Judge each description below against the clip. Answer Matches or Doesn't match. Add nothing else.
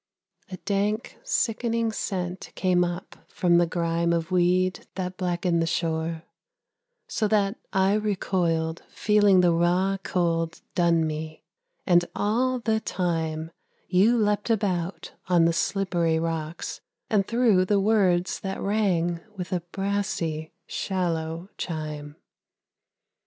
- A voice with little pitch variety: Doesn't match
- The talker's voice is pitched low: Doesn't match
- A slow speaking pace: Matches